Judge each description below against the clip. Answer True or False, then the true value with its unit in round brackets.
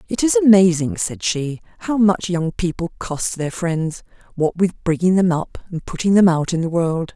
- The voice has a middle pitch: True (175 Hz)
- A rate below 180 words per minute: False (200 wpm)